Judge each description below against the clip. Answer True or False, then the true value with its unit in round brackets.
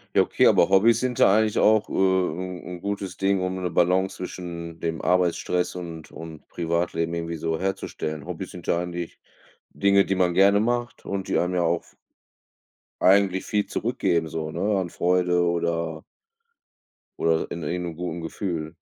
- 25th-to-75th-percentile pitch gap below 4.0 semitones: True (2.5 semitones)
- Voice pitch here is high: False (90 Hz)